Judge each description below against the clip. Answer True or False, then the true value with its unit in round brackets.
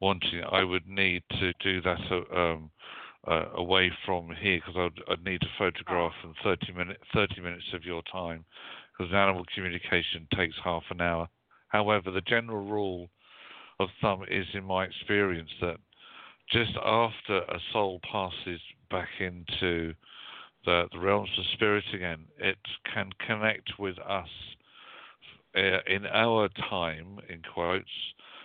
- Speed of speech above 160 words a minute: False (140 wpm)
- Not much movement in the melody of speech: True (2.3 semitones)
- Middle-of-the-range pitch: False (95 Hz)